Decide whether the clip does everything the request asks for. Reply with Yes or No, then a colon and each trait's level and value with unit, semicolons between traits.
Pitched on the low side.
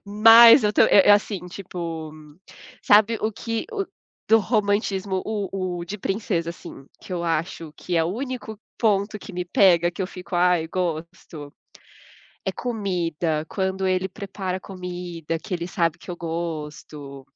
No: medium, 185 Hz